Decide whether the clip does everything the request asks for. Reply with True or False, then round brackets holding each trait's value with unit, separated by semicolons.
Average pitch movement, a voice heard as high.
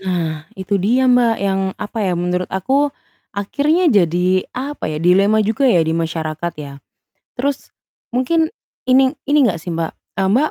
False (6.7 semitones; 195 Hz)